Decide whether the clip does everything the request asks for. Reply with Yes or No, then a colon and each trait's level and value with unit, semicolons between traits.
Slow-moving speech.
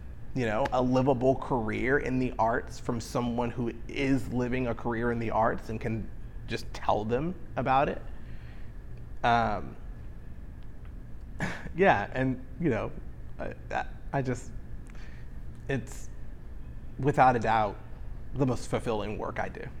Yes: slow, 130 wpm